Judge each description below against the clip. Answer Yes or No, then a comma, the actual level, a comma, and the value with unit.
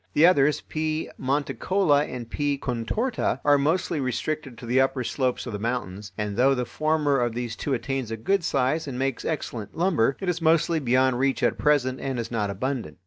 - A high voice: No, low, 135 Hz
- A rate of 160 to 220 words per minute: Yes, average, 200 wpm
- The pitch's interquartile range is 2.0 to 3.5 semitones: No, average, 4.1 semitones